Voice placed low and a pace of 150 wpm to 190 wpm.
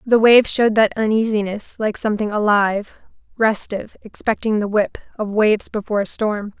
No: high, 210 Hz; average, 155 wpm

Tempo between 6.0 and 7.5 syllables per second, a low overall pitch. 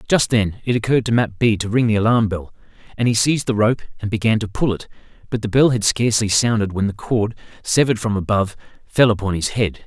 Yes: 6.2 syllables/s; low, 110 Hz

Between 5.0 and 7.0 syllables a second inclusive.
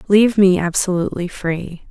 Yes: 5.1 syllables/s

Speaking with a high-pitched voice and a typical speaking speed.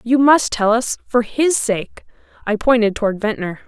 Yes: high, 230 Hz; average, 165 wpm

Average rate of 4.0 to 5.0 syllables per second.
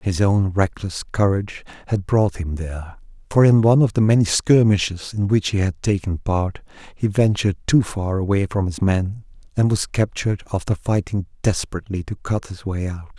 No: 5.3 syllables/s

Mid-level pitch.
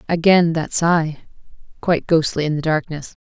Yes: medium, 160 Hz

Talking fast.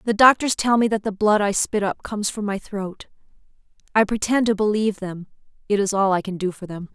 Yes: fast, 235 wpm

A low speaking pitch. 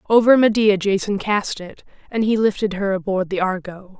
No: high, 200 Hz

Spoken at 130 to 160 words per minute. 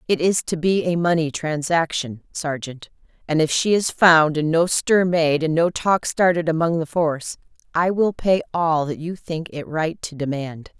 No: average, 195 wpm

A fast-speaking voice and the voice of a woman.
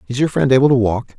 No: fast, 305 wpm; male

